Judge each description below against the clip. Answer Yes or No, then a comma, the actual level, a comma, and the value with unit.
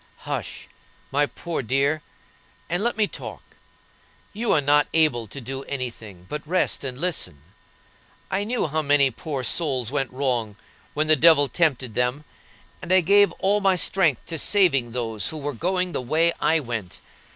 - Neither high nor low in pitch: Yes, medium, 145 Hz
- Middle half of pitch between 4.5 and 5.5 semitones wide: Yes, average, 5.1 semitones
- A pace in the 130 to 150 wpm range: No, average, 170 wpm